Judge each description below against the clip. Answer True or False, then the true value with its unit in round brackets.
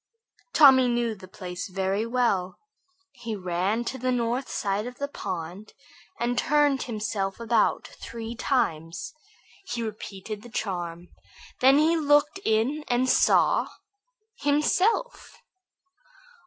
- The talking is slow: True (115 wpm)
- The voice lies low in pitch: False (230 Hz)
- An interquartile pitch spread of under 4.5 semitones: False (5.3 semitones)